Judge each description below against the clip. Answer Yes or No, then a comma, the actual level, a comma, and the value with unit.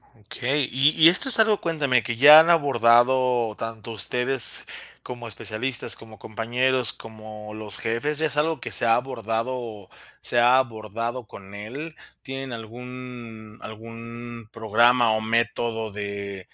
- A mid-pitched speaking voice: No, low, 120 Hz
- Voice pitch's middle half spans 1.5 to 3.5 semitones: Yes, average, 2.9 semitones